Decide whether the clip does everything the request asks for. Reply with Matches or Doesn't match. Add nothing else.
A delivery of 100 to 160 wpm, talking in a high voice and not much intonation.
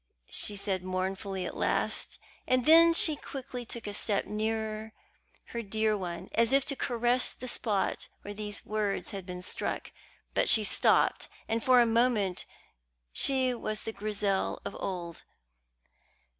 Doesn't match